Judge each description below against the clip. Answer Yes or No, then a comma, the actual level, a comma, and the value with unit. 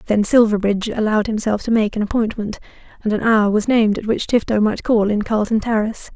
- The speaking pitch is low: No, high, 215 Hz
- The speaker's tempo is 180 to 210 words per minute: Yes, fast, 205 wpm